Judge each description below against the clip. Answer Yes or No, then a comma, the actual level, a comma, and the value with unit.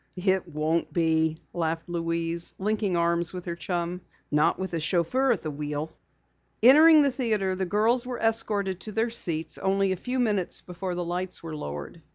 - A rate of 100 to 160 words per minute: No, average, 180 wpm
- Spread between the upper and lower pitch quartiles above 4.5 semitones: No, average, 4.2 semitones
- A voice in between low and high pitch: Yes, medium, 180 Hz